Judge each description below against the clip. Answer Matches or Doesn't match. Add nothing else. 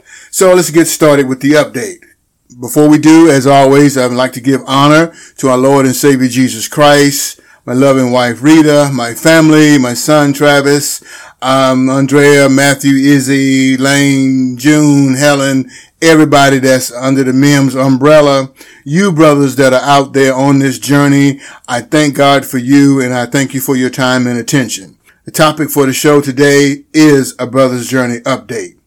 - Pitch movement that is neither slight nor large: Doesn't match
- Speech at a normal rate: Matches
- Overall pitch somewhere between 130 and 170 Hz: Matches